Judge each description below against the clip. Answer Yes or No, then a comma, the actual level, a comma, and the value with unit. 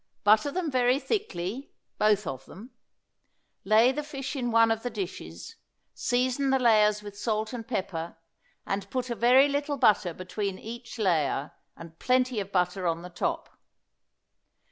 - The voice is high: Yes, high, 220 Hz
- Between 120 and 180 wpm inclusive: Yes, average, 155 wpm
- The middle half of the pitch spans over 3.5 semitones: Yes, average, 5.1 semitones